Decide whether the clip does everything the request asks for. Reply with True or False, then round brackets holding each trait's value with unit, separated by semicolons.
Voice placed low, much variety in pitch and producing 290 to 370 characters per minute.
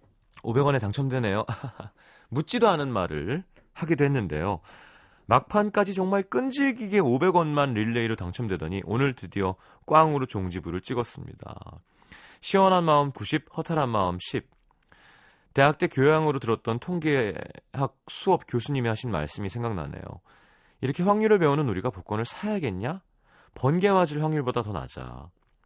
True (130 Hz; 7.0 semitones; 300 characters per minute)